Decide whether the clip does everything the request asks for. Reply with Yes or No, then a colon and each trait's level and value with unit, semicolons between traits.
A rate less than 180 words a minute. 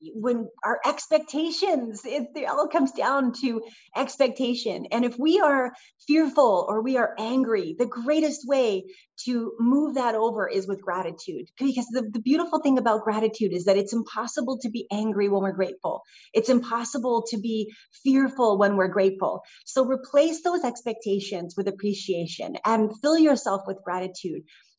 Yes: average, 155 wpm